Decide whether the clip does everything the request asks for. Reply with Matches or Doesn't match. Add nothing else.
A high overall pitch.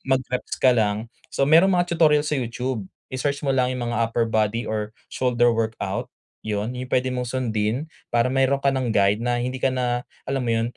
Doesn't match